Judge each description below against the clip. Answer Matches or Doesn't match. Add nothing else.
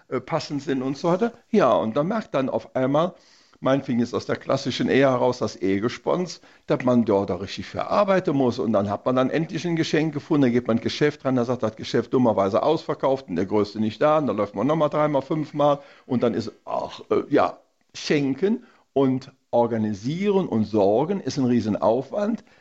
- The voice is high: Doesn't match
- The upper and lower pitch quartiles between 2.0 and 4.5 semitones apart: Doesn't match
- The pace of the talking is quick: Matches